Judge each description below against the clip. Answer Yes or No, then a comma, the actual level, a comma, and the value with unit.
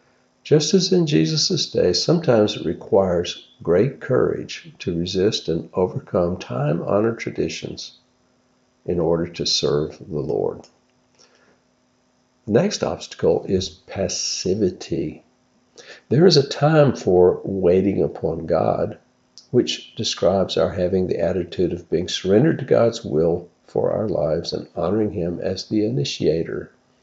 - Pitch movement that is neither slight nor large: No, wide, 6.7 semitones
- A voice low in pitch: Yes, very low, 95 Hz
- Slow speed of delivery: Yes, slow, 125 wpm